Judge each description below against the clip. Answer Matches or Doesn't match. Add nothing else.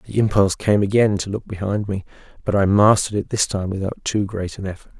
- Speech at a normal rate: Doesn't match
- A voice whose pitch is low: Matches